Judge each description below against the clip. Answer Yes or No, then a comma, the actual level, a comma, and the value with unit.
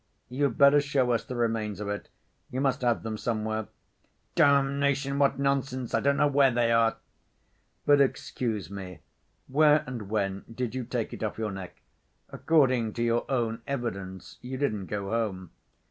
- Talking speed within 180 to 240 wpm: No, average, 165 wpm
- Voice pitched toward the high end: No, low, 120 Hz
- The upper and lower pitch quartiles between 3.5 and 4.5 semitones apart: Yes, average, 4.2 semitones